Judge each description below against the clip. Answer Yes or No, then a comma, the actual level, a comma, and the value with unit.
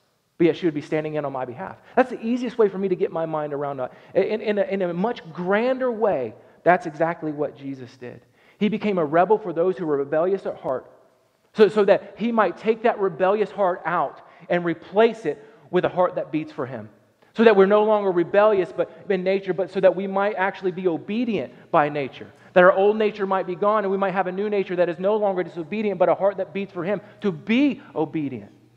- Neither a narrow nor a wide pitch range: Yes, average, 4.2 semitones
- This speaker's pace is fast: Yes, fast, 235 wpm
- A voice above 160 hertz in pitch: Yes, high, 190 Hz